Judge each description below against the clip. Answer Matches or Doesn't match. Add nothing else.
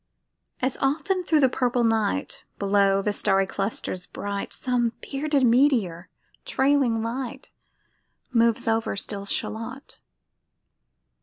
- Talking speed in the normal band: Doesn't match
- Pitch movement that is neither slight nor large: Matches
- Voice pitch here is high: Matches